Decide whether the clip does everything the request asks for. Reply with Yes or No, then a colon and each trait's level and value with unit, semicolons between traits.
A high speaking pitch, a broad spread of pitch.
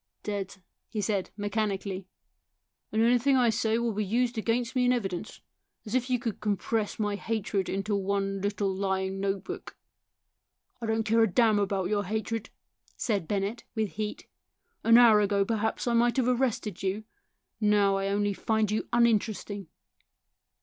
No: high, 210 Hz; narrow, 2.5 semitones